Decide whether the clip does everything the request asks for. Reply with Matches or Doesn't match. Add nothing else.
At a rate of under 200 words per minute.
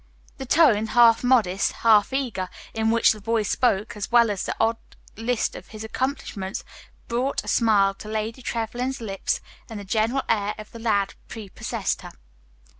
Matches